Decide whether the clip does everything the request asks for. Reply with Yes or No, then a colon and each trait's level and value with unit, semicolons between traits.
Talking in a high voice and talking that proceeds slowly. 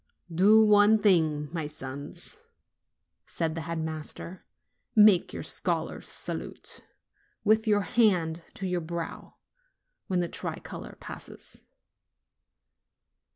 No: medium, 175 Hz; slow, 105 wpm